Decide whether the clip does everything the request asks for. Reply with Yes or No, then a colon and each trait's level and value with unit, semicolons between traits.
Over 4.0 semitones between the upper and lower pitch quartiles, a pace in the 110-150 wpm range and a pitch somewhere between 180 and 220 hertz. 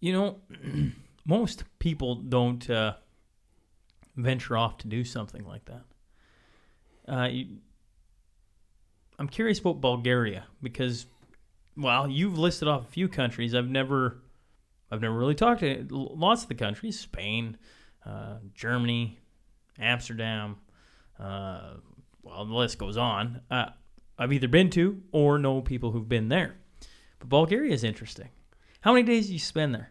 No: average, 5.1 semitones; average, 140 wpm; low, 125 Hz